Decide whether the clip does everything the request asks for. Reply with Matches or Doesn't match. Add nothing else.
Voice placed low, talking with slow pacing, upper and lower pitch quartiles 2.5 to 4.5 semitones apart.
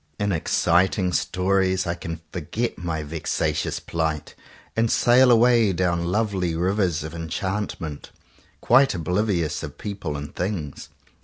Matches